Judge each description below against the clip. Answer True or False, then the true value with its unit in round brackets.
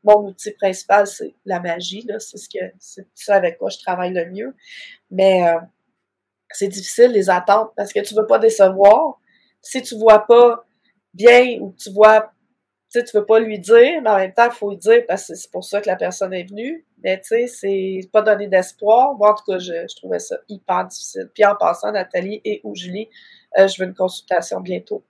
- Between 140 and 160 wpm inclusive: False (215 wpm)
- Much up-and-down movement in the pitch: False (3.6 semitones)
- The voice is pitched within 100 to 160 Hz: False (210 Hz)